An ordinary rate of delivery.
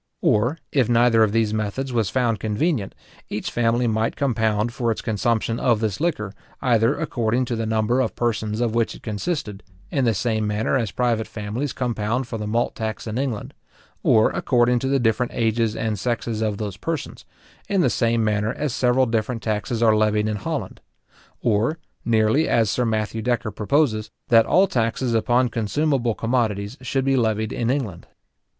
Yes: average, 180 wpm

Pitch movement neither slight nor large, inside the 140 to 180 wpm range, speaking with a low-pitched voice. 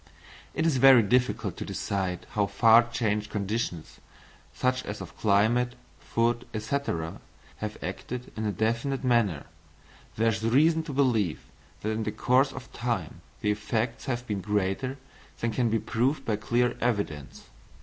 Yes: average, 3.1 semitones; average, 150 wpm; low, 115 Hz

